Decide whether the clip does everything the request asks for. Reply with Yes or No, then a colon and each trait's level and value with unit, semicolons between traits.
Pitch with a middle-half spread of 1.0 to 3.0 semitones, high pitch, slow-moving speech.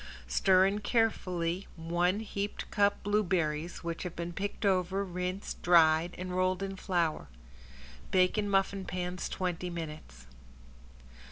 No: narrow, 2.4 semitones; medium, 180 Hz; slow, 125 wpm